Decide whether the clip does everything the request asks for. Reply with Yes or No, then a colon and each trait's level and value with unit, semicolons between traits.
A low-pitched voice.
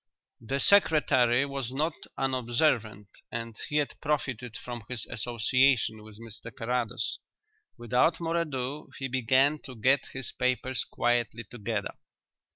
Yes: low, 125 Hz